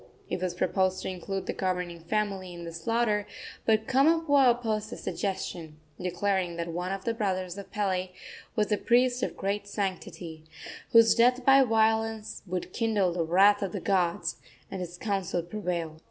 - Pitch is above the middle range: Yes, high, 195 Hz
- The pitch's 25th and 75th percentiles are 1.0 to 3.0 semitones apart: No, average, 3.7 semitones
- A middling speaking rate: Yes, average, 170 wpm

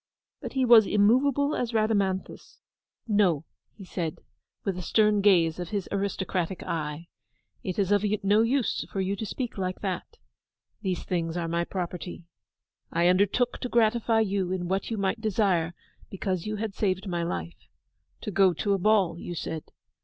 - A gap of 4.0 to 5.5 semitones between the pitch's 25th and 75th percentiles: No, average, 3.5 semitones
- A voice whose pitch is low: No, high, 195 Hz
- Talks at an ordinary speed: Yes, average, 170 wpm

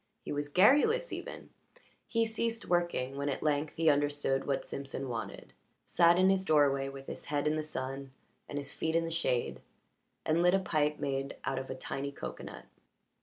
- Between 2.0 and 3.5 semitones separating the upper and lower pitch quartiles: No, average, 4.0 semitones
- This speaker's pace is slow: No, average, 185 wpm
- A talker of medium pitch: Yes, medium, 145 Hz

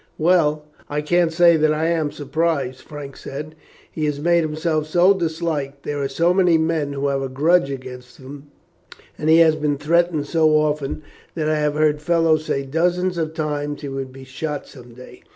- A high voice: No, medium, 150 Hz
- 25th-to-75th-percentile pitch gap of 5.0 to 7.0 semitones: No, narrow, 2.5 semitones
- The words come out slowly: No, average, 190 wpm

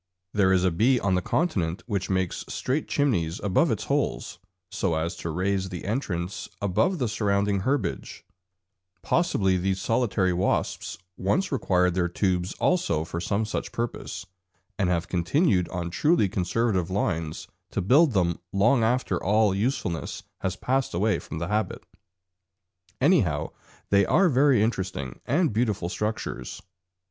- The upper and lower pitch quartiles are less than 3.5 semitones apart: No, average, 4.8 semitones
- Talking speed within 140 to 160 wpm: Yes, average, 145 wpm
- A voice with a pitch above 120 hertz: No, low, 100 Hz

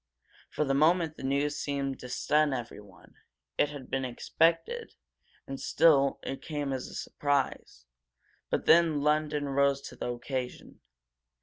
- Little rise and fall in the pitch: Yes, narrow, 2.2 semitones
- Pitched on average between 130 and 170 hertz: Yes, medium, 140 Hz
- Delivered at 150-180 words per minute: No, average, 140 wpm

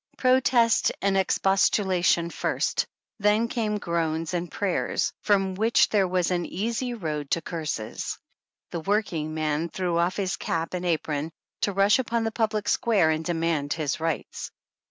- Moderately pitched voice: Yes, medium, 180 Hz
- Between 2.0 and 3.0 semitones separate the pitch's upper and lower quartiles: No, average, 4.2 semitones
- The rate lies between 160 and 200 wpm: No, average, 150 wpm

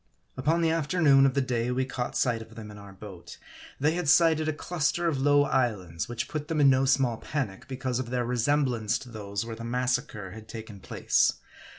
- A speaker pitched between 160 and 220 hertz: No, low, 125 Hz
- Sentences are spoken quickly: Yes, fast, 215 wpm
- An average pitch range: Yes, average, 4.4 semitones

